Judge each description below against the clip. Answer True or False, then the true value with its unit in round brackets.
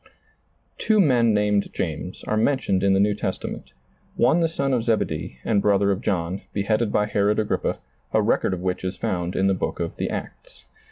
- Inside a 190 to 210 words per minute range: True (200 wpm)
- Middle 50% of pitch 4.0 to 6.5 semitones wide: False (3.4 semitones)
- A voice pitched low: True (105 Hz)